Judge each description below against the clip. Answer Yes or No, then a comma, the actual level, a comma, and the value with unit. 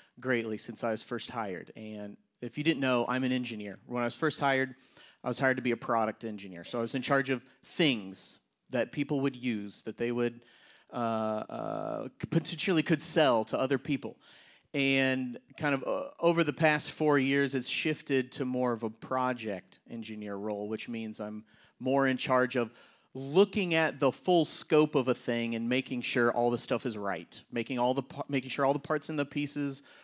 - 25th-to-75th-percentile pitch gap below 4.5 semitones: Yes, average, 3.6 semitones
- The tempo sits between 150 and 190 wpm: No, average, 200 wpm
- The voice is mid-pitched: No, low, 130 Hz